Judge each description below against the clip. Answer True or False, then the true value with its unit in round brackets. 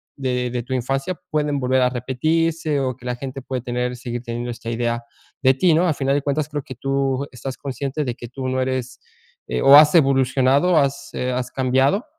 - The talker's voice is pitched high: False (130 Hz)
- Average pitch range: False (2.2 semitones)